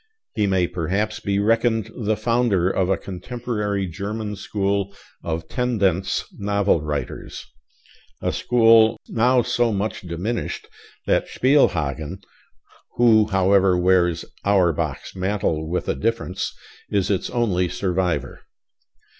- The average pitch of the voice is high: No, low, 100 Hz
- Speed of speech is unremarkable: No, slow, 115 wpm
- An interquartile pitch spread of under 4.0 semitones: Yes, average, 3.5 semitones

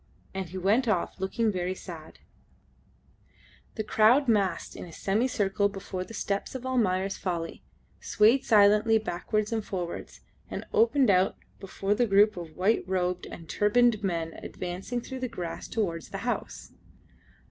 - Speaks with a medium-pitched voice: No, high, 200 Hz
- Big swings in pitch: No, average, 3.5 semitones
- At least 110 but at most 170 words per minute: Yes, average, 145 wpm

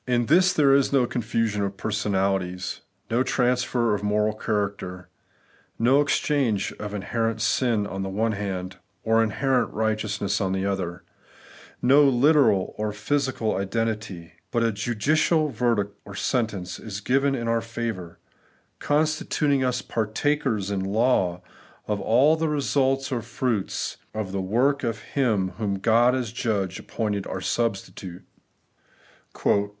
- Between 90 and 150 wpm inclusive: Yes, slow, 135 wpm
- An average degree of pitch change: Yes, average, 4.2 semitones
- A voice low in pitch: Yes, low, 110 Hz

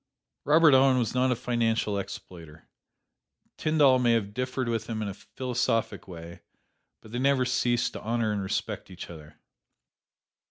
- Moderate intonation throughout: Yes, average, 4.0 semitones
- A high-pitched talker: No, low, 115 Hz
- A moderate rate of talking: Yes, average, 155 wpm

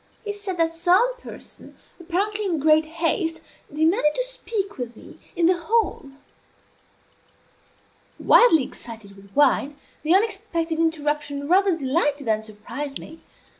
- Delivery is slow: Yes, slow, 130 wpm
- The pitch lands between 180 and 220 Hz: No, very high, 325 Hz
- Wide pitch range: No, average, 4.8 semitones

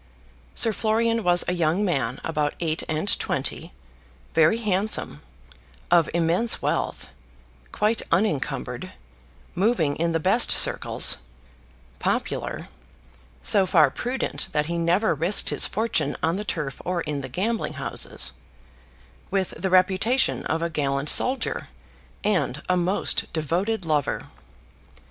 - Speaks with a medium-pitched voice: Yes, medium, 175 Hz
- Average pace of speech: No, slow, 120 wpm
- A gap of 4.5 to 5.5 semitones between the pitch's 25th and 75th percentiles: Yes, average, 4.9 semitones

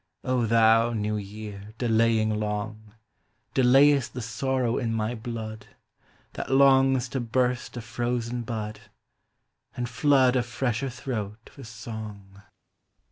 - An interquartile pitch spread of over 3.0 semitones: No, narrow, 2.5 semitones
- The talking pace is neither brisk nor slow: No, slow, 120 wpm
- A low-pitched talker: Yes, low, 115 Hz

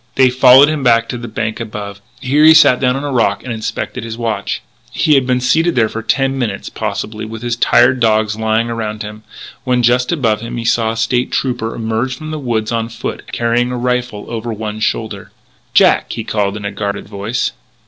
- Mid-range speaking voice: No, low, 115 Hz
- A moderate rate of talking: No, fast, 210 wpm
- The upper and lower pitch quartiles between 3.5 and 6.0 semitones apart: No, narrow, 2.5 semitones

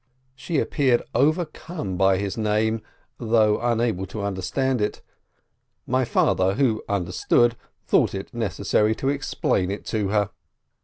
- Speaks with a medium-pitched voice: No, low, 110 Hz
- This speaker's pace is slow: Yes, slow, 125 wpm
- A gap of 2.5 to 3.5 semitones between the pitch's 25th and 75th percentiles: No, average, 4.4 semitones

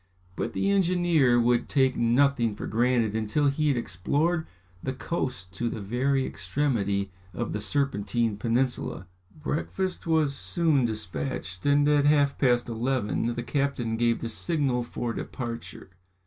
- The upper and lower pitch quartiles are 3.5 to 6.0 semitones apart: Yes, average, 3.8 semitones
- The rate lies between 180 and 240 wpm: No, average, 140 wpm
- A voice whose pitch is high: No, low, 125 Hz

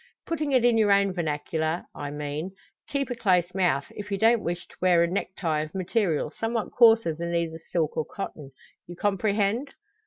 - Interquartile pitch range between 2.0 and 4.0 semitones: No, average, 5.3 semitones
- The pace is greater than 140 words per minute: Yes, average, 185 wpm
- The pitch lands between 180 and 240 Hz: Yes, medium, 185 Hz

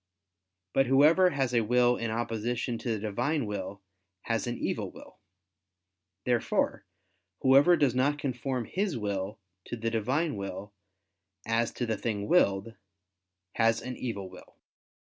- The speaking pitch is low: Yes, low, 120 Hz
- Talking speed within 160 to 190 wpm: No, average, 140 wpm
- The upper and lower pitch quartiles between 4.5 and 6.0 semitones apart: No, average, 3.7 semitones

